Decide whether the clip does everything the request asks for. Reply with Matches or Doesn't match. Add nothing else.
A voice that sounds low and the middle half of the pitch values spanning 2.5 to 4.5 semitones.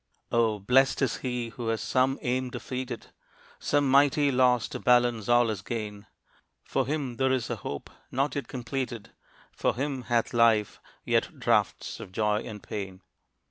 Matches